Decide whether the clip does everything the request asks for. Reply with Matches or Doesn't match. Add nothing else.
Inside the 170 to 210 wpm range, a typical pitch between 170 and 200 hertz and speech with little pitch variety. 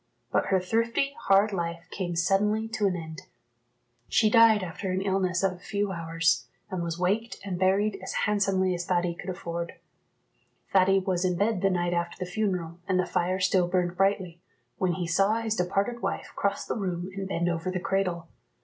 Matches